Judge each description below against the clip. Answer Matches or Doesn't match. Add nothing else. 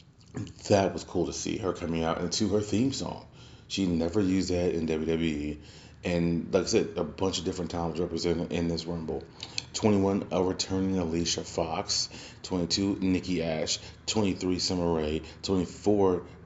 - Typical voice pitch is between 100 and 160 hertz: Doesn't match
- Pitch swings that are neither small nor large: Doesn't match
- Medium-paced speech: Matches